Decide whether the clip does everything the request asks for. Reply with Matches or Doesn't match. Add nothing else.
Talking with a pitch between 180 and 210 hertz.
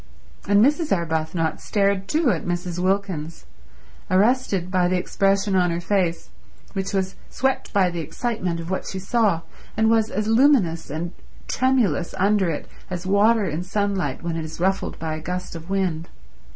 Matches